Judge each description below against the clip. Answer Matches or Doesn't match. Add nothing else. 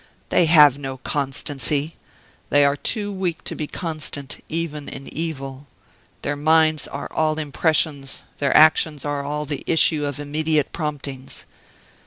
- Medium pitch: Matches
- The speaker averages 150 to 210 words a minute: Doesn't match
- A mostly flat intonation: Matches